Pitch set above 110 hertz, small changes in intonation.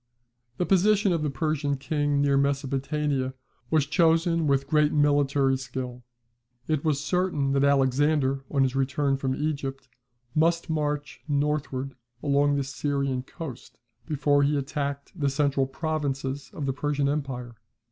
Yes: medium, 140 Hz; narrow, 1.8 semitones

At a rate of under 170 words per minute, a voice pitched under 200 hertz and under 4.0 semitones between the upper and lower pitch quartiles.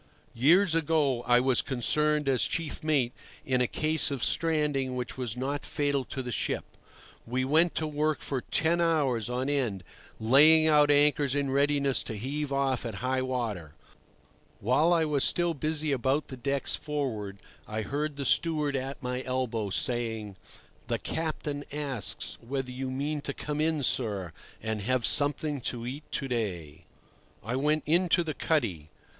Yes: average, 160 wpm; low, 135 Hz; average, 3.4 semitones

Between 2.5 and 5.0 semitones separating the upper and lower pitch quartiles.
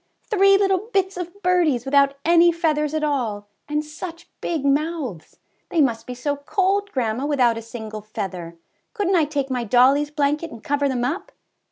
No: wide, 5.5 semitones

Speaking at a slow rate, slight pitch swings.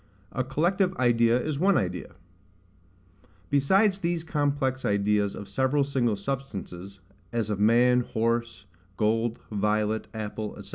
No: slow, 125 wpm; average, 4.9 semitones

